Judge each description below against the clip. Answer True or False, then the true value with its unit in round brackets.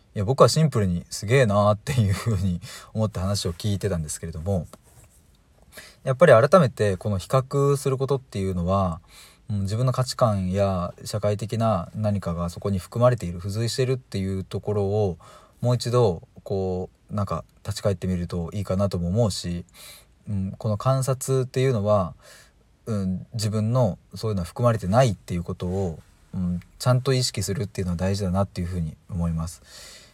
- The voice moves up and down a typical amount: True (4.5 semitones)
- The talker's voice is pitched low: True (100 Hz)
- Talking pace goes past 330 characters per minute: True (375 characters per minute)